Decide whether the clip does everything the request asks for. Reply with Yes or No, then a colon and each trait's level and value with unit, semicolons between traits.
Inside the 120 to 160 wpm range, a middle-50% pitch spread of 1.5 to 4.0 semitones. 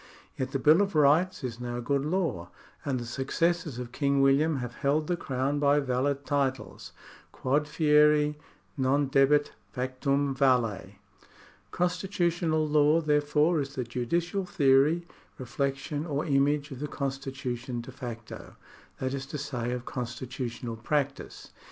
Yes: average, 140 wpm; average, 2.7 semitones